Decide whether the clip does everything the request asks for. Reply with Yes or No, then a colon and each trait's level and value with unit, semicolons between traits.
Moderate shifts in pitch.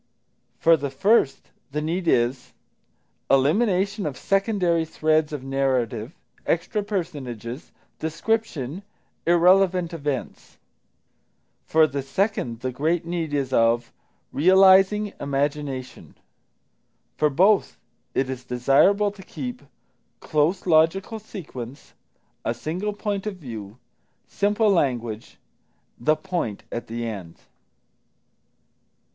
No: wide, 6.5 semitones